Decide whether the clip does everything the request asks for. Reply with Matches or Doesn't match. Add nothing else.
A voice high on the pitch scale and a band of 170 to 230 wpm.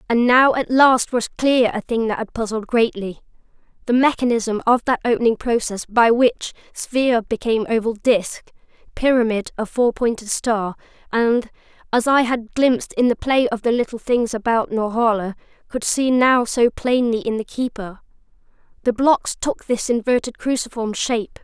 Doesn't match